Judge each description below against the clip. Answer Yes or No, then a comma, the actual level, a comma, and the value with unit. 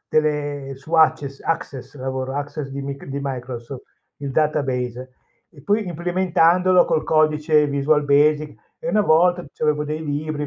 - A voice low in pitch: No, medium, 150 Hz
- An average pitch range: No, narrow, 2.3 semitones